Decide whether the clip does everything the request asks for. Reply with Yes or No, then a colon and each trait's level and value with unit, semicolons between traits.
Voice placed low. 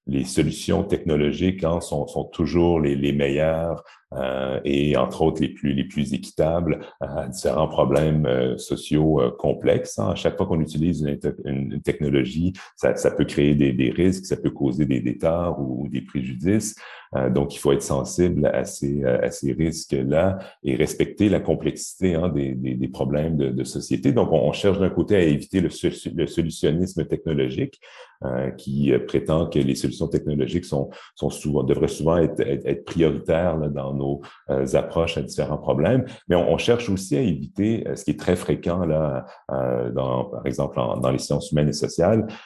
Yes: very low, 75 Hz